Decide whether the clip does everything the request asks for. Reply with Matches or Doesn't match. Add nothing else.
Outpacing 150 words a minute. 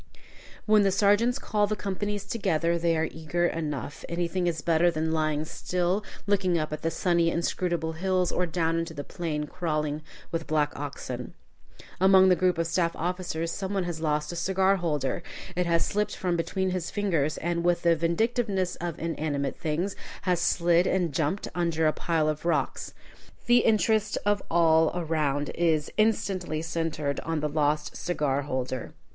Matches